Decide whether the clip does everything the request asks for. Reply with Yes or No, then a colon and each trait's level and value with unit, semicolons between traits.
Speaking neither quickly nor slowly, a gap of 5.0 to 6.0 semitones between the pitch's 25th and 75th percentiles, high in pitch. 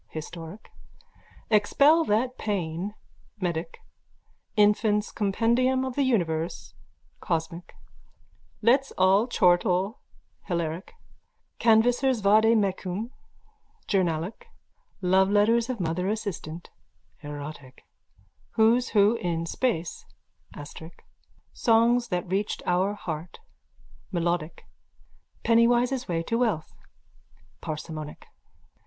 No: slow, 85 wpm; average, 5.3 semitones; high, 200 Hz